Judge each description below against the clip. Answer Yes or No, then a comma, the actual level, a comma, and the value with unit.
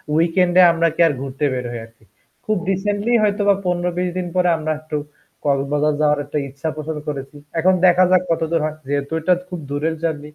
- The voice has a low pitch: No, medium, 160 Hz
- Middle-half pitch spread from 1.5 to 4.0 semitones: Yes, average, 3.6 semitones